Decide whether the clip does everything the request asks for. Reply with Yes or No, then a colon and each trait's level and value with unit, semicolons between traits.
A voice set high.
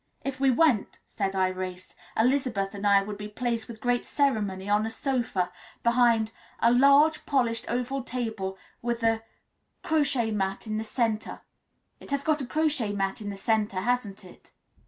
Yes: high, 225 Hz